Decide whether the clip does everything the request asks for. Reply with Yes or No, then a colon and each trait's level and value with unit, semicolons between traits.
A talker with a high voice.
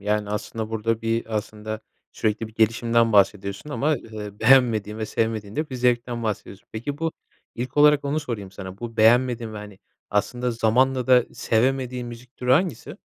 No: low, 115 Hz